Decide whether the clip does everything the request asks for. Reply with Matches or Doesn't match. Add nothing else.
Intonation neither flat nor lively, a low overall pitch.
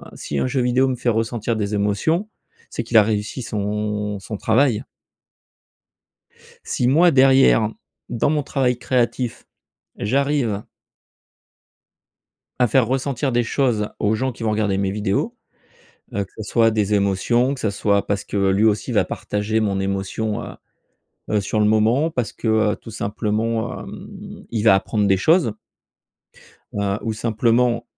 Matches